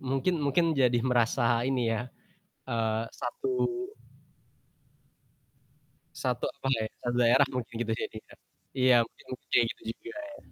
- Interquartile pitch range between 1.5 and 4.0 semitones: Yes, average, 2.7 semitones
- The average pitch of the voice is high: No, low, 125 Hz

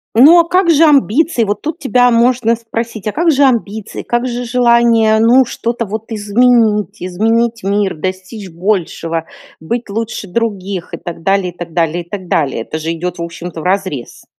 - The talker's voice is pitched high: Yes, high, 220 Hz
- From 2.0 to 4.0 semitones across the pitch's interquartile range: No, average, 4.5 semitones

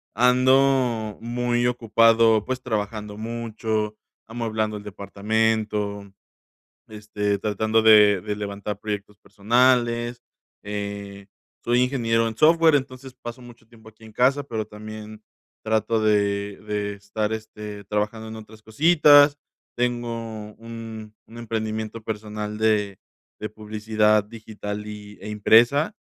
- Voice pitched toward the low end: Yes, low, 110 Hz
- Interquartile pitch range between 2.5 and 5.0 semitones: No, narrow, 1.9 semitones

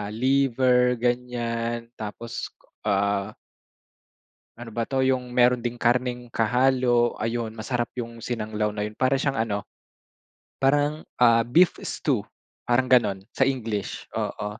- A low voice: Yes, low, 120 Hz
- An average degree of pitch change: No, narrow, 1.8 semitones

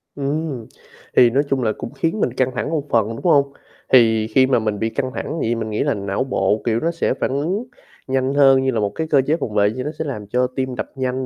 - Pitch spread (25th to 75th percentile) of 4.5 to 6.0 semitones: No, average, 3.8 semitones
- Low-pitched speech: Yes, low, 130 Hz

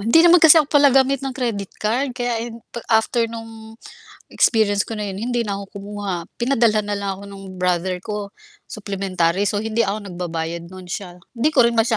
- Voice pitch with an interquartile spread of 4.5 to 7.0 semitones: No, average, 3.4 semitones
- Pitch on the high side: Yes, high, 215 Hz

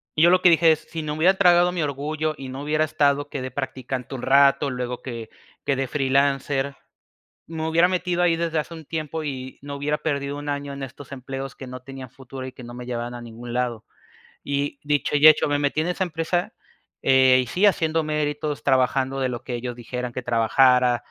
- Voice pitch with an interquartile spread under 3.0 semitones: No, average, 3.3 semitones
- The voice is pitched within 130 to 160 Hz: Yes, medium, 140 Hz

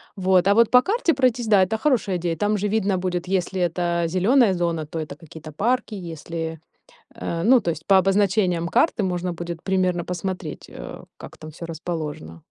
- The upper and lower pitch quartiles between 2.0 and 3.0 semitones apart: No, average, 3.6 semitones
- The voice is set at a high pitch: No, medium, 180 Hz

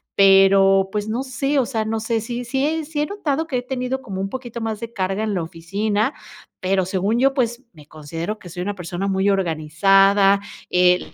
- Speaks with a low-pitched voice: No, high, 205 Hz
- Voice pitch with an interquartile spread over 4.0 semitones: Yes, average, 4.5 semitones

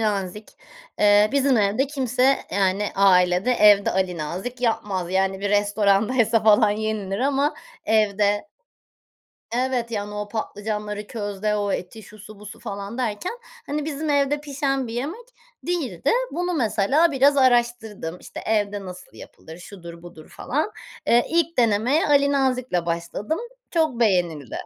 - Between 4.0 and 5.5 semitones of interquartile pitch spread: Yes, average, 4.7 semitones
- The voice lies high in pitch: Yes, high, 215 Hz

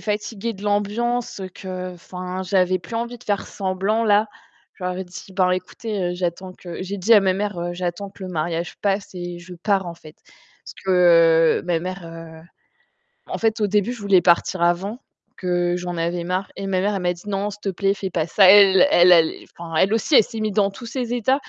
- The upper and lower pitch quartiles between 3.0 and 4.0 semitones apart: No, narrow, 2.6 semitones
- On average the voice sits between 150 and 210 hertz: Yes, high, 190 Hz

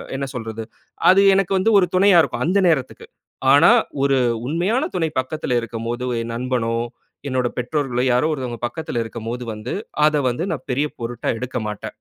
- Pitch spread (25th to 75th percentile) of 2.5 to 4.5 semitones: No, average, 4.9 semitones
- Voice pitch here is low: Yes, low, 130 Hz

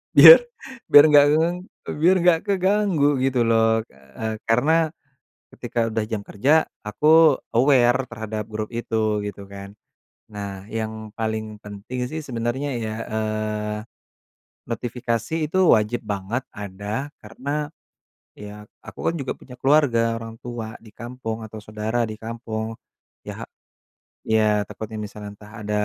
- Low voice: Yes, low, 115 Hz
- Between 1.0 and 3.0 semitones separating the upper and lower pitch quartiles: No, average, 3.6 semitones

